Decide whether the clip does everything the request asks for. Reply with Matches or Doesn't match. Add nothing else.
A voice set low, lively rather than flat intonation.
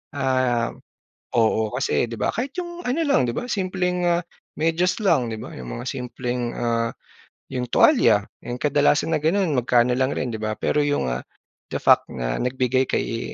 Matches